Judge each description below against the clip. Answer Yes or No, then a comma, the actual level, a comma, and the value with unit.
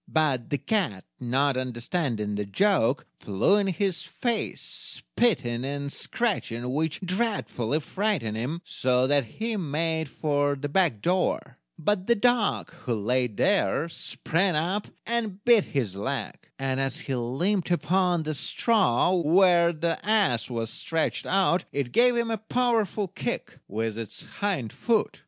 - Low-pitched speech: No, medium, 160 Hz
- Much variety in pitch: Yes, wide, 7.7 semitones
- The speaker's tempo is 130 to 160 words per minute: Yes, average, 145 wpm